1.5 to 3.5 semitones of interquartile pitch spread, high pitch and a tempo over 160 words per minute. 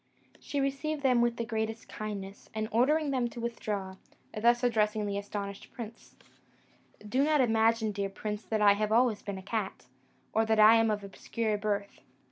Yes: narrow, 2.5 semitones; high, 220 Hz; average, 175 wpm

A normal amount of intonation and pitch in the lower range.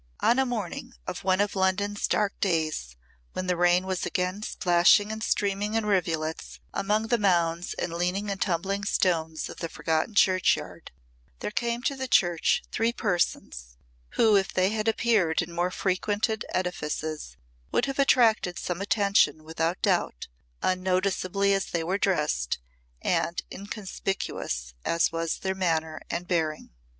No: average, 3.4 semitones; medium, 185 Hz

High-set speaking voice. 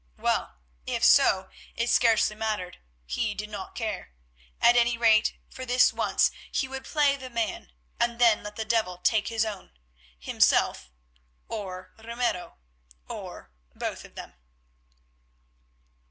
Yes: high, 220 Hz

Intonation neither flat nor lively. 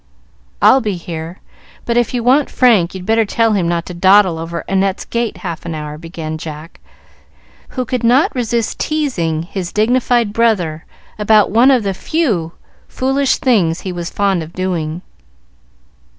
No: wide, 5.8 semitones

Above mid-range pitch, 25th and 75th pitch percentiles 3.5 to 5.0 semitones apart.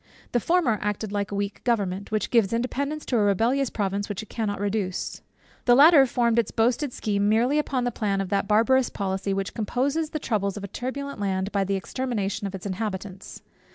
Yes: high, 215 Hz; average, 3.9 semitones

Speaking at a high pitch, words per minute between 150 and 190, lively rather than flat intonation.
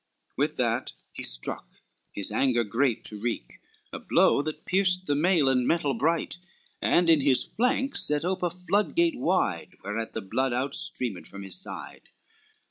No: medium, 140 Hz; average, 165 wpm; wide, 7.7 semitones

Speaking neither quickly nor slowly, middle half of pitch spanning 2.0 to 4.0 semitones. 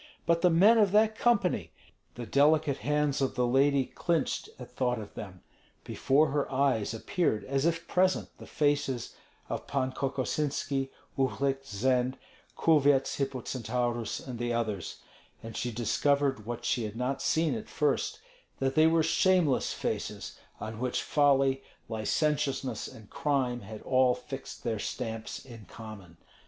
Yes: average, 145 wpm; average, 3.7 semitones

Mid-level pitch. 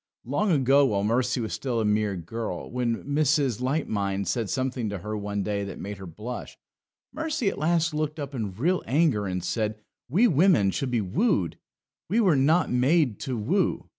No: low, 125 Hz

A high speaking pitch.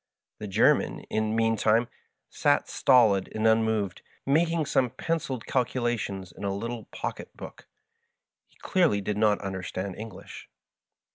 No: low, 110 Hz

